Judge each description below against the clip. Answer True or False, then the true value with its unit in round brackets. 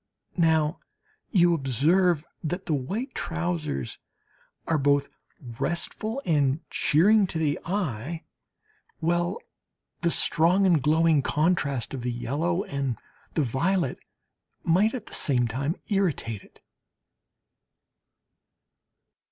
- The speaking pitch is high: False (160 Hz)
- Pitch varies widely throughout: False (4.3 semitones)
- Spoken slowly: True (105 wpm)